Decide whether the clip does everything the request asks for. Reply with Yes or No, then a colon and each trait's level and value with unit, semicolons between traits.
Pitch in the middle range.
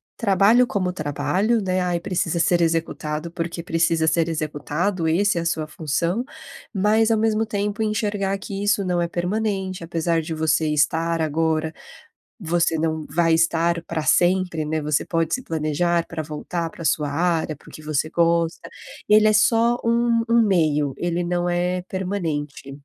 Yes: medium, 170 Hz